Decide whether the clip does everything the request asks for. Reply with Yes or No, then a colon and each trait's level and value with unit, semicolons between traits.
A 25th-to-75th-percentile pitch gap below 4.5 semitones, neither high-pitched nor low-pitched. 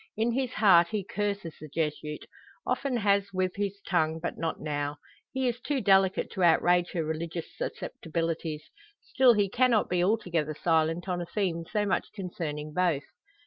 Yes: average, 4.0 semitones; medium, 180 Hz